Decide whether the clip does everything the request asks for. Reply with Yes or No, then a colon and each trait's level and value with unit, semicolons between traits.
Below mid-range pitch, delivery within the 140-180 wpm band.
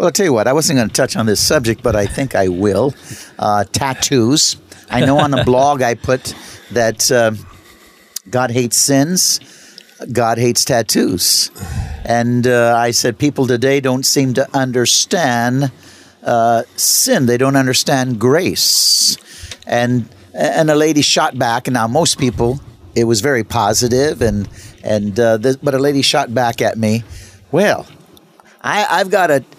Yes: low, 120 Hz; average, 165 wpm